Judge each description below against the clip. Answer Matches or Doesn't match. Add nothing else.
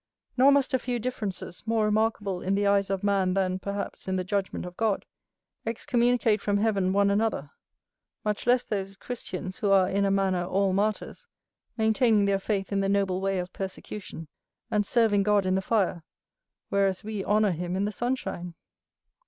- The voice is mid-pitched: Doesn't match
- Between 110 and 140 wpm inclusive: Doesn't match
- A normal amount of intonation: Doesn't match